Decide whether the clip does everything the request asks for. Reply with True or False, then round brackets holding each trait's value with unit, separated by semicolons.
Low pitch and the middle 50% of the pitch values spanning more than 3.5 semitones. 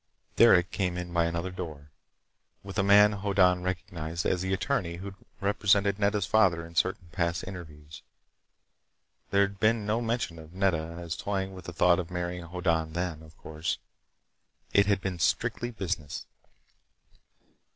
False (90 Hz; 2.8 semitones)